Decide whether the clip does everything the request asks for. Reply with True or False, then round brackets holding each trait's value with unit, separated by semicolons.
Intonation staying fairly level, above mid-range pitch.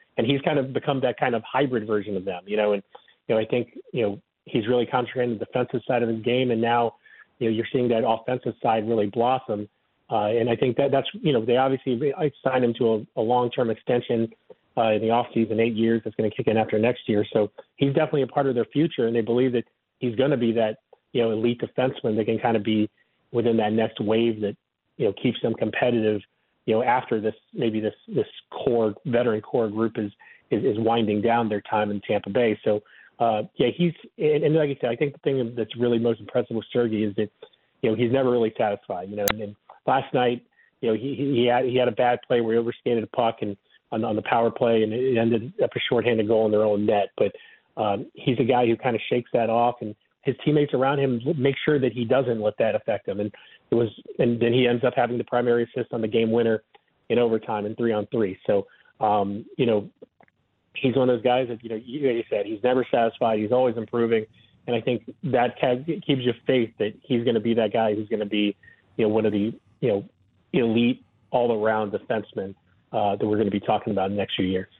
False (2.3 semitones; 115 Hz)